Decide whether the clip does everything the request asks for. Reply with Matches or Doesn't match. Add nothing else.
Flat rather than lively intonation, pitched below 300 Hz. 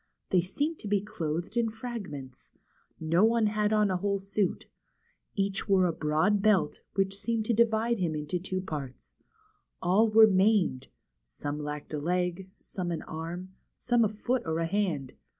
Doesn't match